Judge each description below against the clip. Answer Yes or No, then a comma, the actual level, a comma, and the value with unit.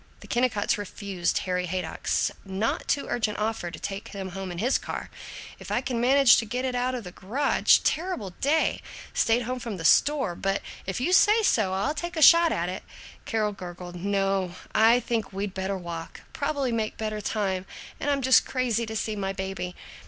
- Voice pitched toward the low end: No, high, 215 Hz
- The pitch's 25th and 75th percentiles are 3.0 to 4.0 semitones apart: No, average, 4.9 semitones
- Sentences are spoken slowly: No, average, 195 wpm